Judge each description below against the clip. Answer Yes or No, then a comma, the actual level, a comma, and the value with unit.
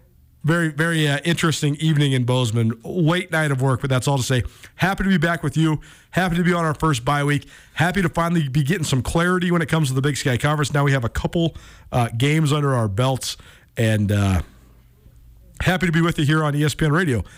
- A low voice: No, medium, 145 Hz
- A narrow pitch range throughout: No, average, 4.8 semitones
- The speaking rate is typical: No, fast, 230 wpm